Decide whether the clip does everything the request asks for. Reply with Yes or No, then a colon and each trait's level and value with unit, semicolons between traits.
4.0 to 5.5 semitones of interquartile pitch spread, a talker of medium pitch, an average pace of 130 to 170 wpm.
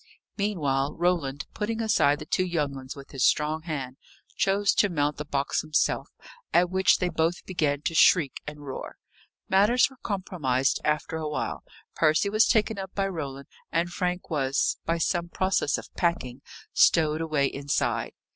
Yes: average, 4.5 semitones; medium, 160 Hz; average, 165 wpm